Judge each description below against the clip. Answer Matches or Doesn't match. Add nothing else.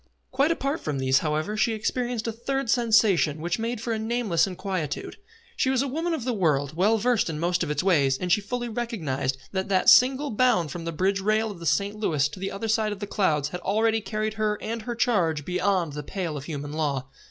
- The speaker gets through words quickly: Matches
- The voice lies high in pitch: Matches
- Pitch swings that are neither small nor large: Doesn't match